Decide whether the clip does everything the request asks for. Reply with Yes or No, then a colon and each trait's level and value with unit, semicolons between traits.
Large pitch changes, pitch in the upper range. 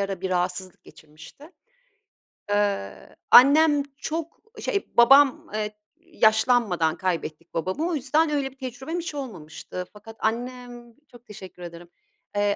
Yes: wide, 6.9 semitones; high, 225 Hz